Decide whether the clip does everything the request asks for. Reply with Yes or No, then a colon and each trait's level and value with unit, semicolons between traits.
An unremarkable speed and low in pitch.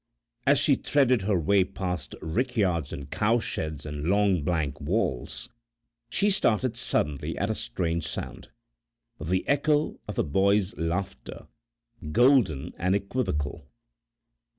No: slow, 120 wpm; very low, 95 Hz